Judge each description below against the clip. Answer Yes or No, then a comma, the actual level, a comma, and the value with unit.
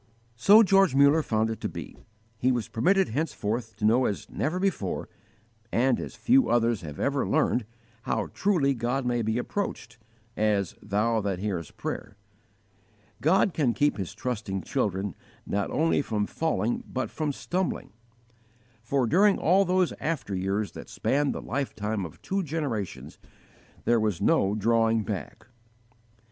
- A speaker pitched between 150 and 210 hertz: No, low, 120 Hz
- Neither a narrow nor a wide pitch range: No, wide, 6.4 semitones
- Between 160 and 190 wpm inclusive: No, average, 150 wpm